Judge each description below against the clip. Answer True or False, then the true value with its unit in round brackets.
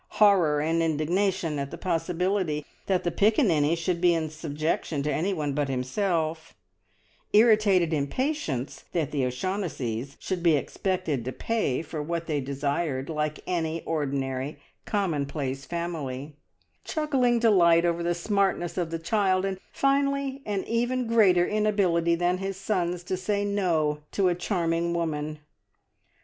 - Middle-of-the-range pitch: True (170 Hz)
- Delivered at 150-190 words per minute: False (135 wpm)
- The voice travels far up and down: False (4.4 semitones)